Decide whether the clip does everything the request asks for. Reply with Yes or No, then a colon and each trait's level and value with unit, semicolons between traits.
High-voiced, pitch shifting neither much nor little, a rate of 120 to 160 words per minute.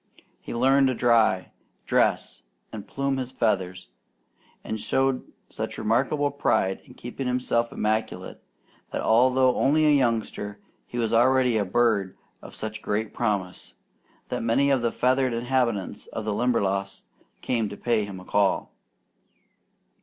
No: low, 115 Hz; average, 3.7 semitones; average, 140 wpm